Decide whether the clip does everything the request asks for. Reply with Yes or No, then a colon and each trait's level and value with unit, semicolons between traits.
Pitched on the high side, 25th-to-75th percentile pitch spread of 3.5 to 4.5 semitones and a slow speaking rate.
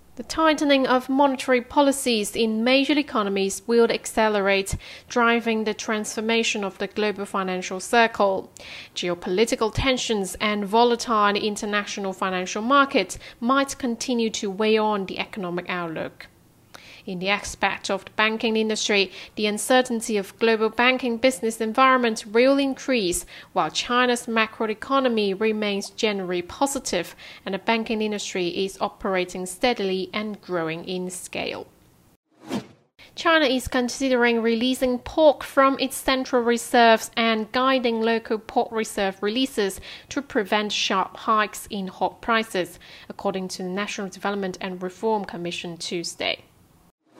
Yes: high, 220 Hz; average, 3.9 semitones; slow, 125 wpm